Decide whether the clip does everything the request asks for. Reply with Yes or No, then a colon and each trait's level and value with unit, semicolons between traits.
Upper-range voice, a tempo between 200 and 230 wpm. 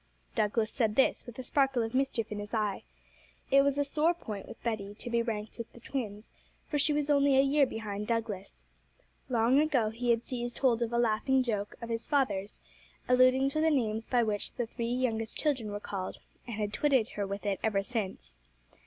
Yes: high, 235 Hz; fast, 205 wpm